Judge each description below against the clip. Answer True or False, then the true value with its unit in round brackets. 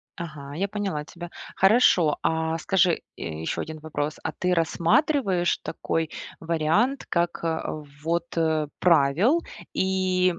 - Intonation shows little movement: False (3.1 semitones)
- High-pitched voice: False (170 Hz)